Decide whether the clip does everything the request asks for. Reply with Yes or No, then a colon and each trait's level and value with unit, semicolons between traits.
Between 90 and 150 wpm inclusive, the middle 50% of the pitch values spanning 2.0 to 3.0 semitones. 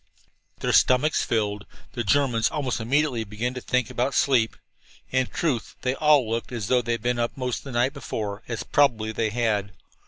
No: average, 190 wpm; average, 2.7 semitones